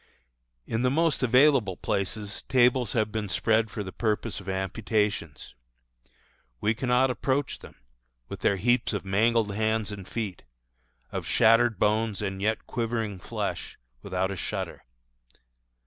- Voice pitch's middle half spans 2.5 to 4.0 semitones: Yes, average, 3.1 semitones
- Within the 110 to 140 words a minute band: Yes, slow, 135 wpm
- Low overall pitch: Yes, low, 110 Hz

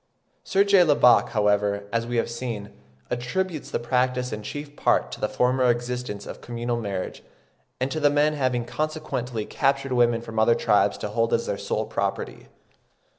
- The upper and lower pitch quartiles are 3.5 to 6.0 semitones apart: No, average, 3.1 semitones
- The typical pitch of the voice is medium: No, low, 120 Hz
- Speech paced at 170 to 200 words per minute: Yes, average, 175 wpm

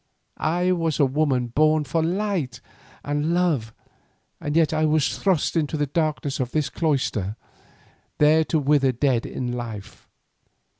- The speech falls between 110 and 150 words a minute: Yes, average, 145 wpm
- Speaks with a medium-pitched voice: Yes, medium, 150 Hz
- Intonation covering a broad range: No, average, 3.5 semitones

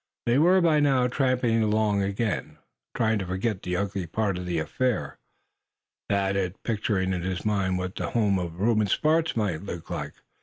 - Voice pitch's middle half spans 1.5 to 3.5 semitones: No, average, 4.0 semitones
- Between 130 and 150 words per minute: No, average, 180 wpm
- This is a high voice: No, low, 100 Hz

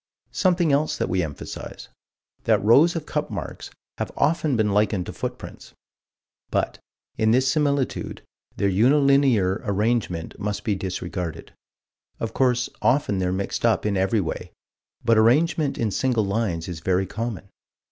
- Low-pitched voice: Yes, low, 110 Hz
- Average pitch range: No, wide, 5.8 semitones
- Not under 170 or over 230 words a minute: No, average, 145 wpm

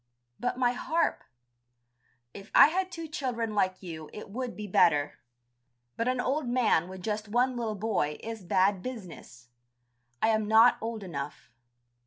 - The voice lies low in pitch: No, high, 220 Hz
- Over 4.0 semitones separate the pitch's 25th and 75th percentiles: Yes, average, 4.9 semitones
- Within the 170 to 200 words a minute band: No, average, 155 wpm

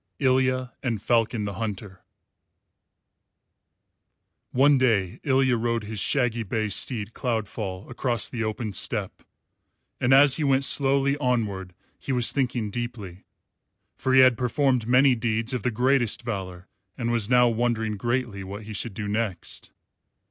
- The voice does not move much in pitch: No, average, 3.3 semitones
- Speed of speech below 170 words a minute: Yes, average, 140 wpm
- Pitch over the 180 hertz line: No, low, 120 Hz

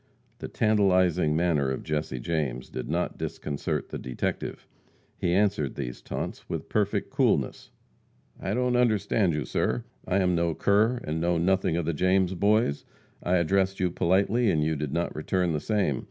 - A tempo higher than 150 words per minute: Yes, average, 170 wpm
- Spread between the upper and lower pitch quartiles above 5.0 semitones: No, average, 4.3 semitones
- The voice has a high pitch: No, very low, 85 Hz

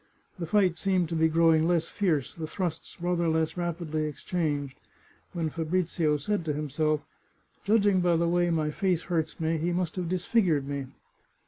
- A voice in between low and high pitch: Yes, medium, 165 Hz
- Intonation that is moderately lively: No, narrow, 2.3 semitones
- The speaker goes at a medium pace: Yes, average, 180 wpm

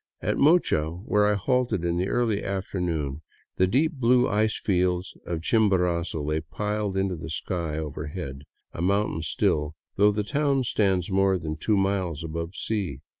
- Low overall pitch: Yes, very low, 95 Hz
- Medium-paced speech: Yes, average, 170 wpm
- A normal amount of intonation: Yes, average, 4.2 semitones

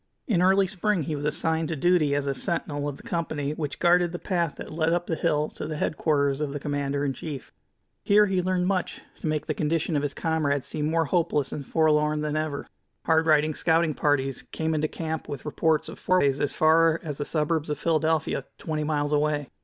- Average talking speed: No, fast, 215 wpm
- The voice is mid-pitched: Yes, medium, 155 Hz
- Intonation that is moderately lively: No, narrow, 2.2 semitones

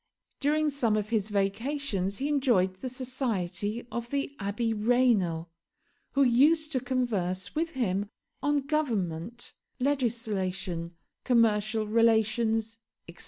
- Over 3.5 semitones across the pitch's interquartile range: Yes, average, 4.6 semitones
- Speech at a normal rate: No, slow, 115 wpm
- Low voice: No, high, 230 Hz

